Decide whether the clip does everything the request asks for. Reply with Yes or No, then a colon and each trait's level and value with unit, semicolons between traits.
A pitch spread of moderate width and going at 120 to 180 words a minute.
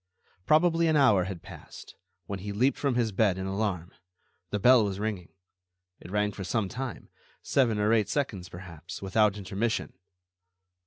Yes: average, 4.0 semitones; average, 160 wpm